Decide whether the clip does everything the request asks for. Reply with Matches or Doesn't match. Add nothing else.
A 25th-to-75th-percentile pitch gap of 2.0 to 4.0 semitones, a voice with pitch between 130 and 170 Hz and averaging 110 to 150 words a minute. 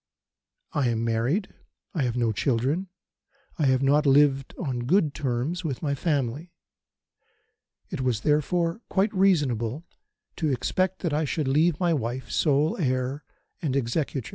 Doesn't match